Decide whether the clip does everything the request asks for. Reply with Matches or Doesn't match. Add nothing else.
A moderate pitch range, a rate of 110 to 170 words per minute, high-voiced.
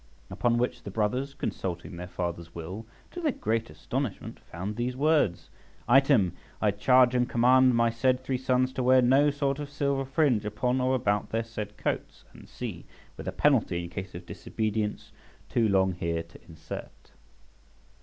Doesn't match